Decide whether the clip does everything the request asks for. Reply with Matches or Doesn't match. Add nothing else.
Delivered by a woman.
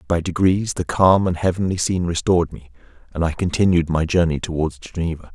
Doesn't match